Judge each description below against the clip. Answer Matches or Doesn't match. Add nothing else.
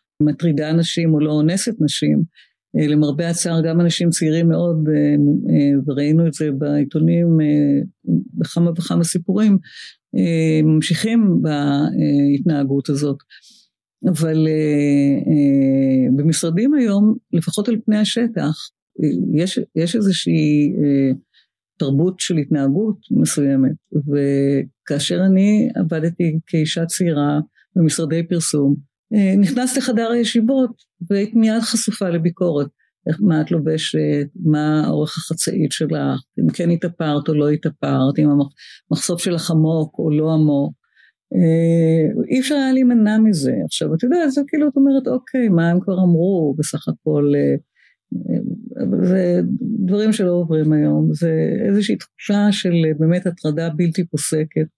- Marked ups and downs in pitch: Doesn't match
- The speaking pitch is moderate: Matches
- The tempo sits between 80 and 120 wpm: Matches